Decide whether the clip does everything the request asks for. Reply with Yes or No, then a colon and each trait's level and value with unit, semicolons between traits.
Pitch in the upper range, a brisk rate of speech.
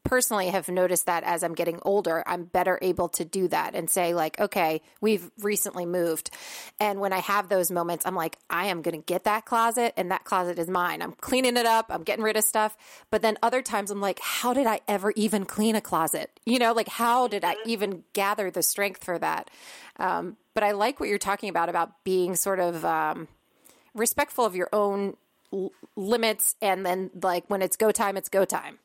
Yes: high, 200 Hz; fast, 220 wpm